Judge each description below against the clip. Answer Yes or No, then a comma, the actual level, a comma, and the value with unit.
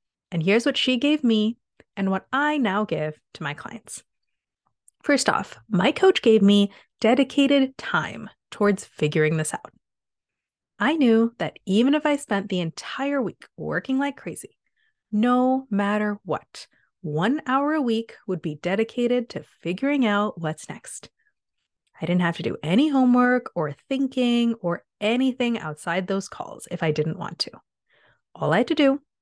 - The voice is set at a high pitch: Yes, high, 225 Hz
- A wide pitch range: Yes, wide, 6.4 semitones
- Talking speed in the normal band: Yes, average, 160 wpm